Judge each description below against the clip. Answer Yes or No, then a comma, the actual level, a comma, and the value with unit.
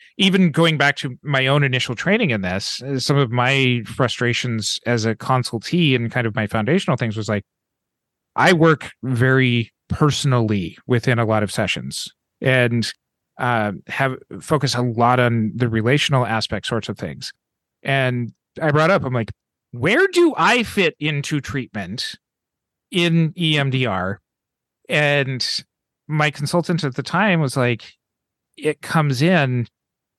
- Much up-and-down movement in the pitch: No, average, 4.5 semitones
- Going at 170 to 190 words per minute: No, average, 145 wpm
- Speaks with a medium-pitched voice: No, low, 130 Hz